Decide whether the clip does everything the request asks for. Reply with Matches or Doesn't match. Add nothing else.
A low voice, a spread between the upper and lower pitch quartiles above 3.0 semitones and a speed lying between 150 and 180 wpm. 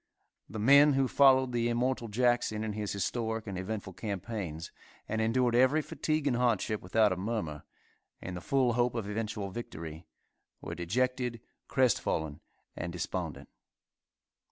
Doesn't match